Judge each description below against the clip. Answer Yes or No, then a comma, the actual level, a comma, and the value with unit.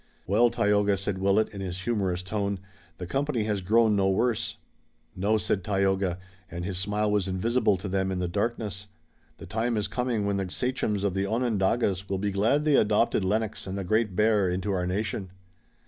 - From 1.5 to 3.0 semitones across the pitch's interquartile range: Yes, narrow, 2.5 semitones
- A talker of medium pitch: No, low, 100 Hz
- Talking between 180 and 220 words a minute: Yes, average, 190 wpm